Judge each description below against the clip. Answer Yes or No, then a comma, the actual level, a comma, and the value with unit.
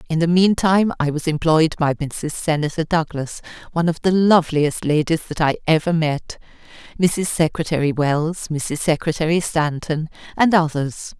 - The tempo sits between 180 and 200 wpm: No, average, 150 wpm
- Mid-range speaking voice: Yes, medium, 160 Hz